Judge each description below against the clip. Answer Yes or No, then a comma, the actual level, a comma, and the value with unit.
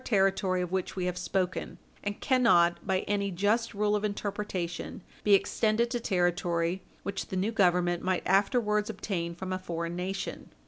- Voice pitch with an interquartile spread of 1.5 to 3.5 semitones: Yes, average, 2.7 semitones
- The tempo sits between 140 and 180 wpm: Yes, average, 170 wpm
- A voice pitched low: No, high, 190 Hz